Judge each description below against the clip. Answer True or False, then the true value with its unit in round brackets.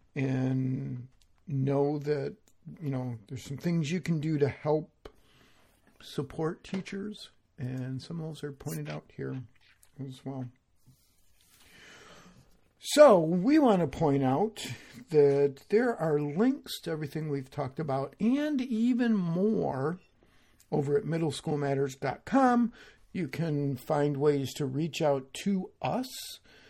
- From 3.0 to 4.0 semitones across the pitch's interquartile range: False (4.6 semitones)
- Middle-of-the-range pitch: True (145 Hz)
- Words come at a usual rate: False (125 wpm)